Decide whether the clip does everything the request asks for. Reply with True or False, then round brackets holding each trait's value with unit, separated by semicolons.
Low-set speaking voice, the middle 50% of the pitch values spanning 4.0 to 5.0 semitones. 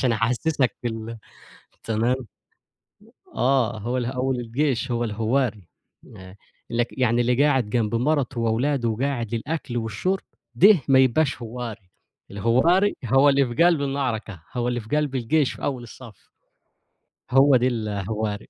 False (120 Hz; 3.2 semitones)